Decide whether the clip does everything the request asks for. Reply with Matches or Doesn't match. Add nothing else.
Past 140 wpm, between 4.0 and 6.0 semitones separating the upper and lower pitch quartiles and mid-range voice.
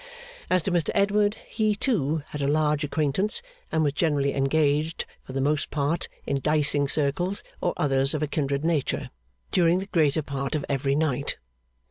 Doesn't match